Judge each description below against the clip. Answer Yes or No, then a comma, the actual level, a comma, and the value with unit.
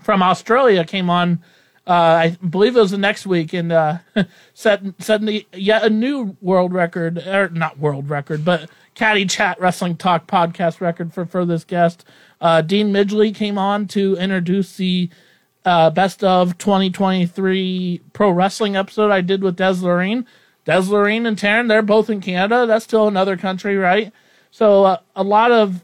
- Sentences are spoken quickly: No, average, 170 wpm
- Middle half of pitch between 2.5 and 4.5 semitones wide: Yes, average, 2.9 semitones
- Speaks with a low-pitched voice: No, high, 190 Hz